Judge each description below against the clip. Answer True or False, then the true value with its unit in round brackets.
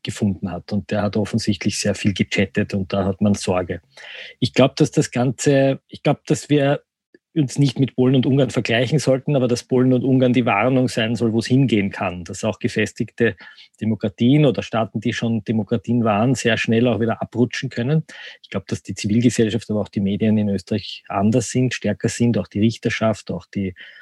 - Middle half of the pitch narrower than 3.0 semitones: False (3.4 semitones)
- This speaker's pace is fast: True (200 wpm)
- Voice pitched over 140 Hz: False (115 Hz)